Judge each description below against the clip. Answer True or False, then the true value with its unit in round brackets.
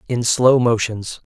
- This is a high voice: False (120 Hz)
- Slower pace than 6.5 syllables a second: True (3.7 syllables/s)